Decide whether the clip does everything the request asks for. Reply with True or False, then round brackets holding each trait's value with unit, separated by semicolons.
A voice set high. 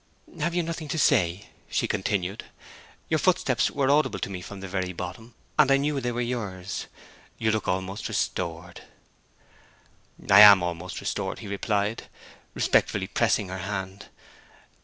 False (100 Hz)